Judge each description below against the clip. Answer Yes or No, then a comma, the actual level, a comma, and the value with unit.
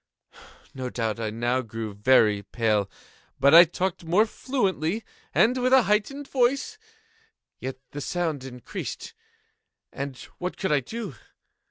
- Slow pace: Yes, slow, 125 wpm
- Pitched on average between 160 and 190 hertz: No, medium, 150 Hz